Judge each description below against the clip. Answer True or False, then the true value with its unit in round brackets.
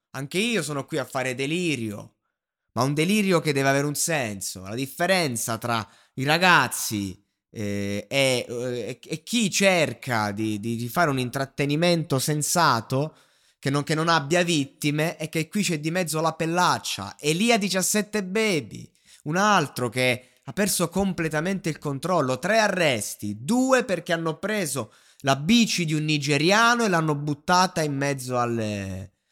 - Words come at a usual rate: True (150 wpm)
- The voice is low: False (150 Hz)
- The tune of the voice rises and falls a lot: True (5.9 semitones)